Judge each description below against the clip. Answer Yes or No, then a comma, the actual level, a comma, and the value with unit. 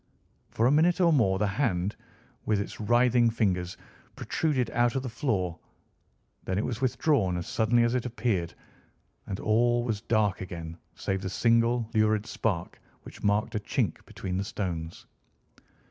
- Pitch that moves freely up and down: No, average, 4.1 semitones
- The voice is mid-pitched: No, low, 110 Hz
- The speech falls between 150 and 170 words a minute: Yes, average, 160 wpm